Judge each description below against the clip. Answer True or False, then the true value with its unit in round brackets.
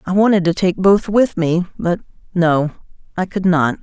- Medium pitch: True (180 Hz)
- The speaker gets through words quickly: False (190 wpm)